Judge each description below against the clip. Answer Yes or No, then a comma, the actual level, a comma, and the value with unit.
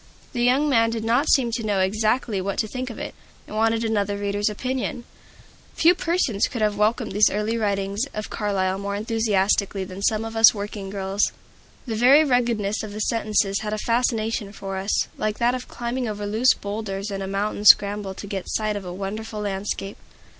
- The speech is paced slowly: No, average, 195 wpm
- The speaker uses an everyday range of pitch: No, narrow, 2.3 semitones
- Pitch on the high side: Yes, high, 215 Hz